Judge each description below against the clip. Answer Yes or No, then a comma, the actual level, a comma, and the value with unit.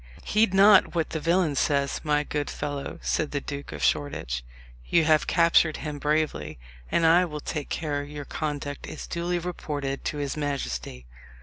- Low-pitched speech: No, medium, 150 Hz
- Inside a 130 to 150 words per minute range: No, average, 170 wpm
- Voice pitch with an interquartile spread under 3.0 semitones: Yes, narrow, 2.5 semitones